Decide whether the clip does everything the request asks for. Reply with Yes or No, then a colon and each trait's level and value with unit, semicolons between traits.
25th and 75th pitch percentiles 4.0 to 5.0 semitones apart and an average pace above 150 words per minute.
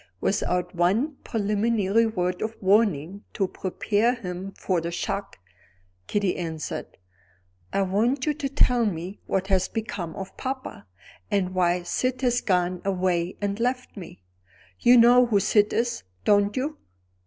No: average, 4.3 semitones; average, 140 wpm